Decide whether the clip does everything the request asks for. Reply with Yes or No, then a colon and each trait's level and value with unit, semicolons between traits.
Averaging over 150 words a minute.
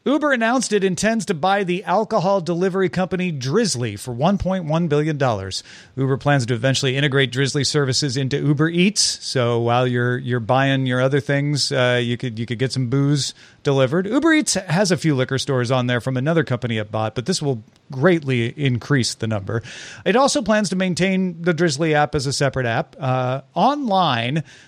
Yes: average, 185 wpm